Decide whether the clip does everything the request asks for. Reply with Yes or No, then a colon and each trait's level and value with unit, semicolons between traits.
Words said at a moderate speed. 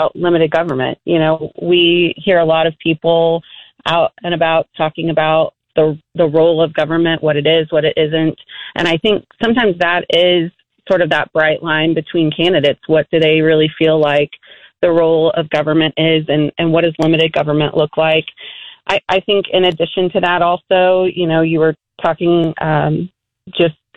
Yes: average, 185 wpm